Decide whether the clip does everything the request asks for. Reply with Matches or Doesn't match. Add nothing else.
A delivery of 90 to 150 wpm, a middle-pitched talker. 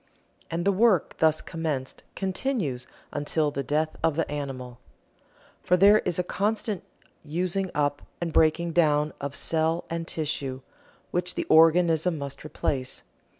Matches